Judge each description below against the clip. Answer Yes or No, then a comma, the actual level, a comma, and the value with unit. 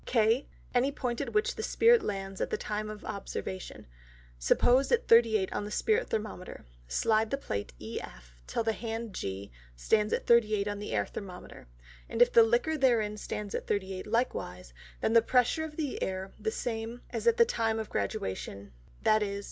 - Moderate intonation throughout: Yes, average, 3.9 semitones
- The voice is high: Yes, high, 220 Hz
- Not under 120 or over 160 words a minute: No, average, 185 wpm